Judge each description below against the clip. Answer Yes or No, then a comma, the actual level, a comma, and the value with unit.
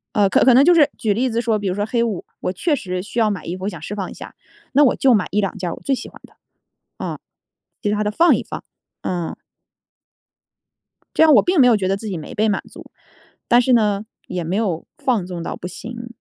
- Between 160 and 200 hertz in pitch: No, high, 210 Hz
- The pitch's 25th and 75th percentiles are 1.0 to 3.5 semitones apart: No, average, 4.3 semitones